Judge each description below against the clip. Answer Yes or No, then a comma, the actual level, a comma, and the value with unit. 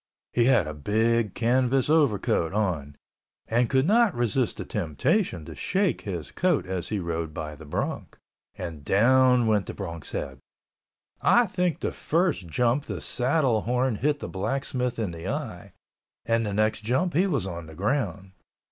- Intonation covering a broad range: Yes, wide, 7.0 semitones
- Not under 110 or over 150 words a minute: No, average, 165 wpm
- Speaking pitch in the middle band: No, low, 115 Hz